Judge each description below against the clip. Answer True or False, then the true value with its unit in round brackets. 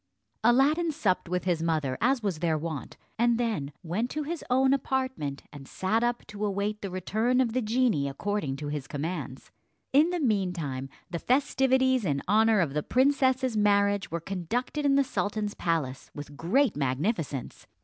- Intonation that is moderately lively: False (8.1 semitones)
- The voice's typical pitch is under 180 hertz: False (205 Hz)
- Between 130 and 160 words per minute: False (170 wpm)